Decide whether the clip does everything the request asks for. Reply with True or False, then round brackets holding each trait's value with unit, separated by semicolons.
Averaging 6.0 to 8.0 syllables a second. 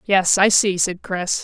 False (3.8 syllables/s)